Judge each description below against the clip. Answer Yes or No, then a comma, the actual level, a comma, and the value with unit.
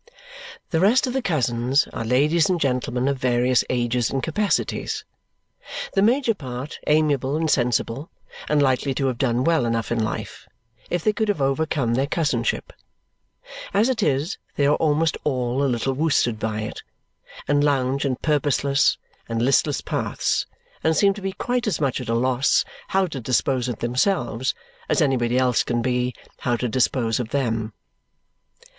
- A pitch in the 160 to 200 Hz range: No, low, 135 Hz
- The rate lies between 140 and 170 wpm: Yes, average, 165 wpm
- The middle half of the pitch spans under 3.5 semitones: No, average, 4.2 semitones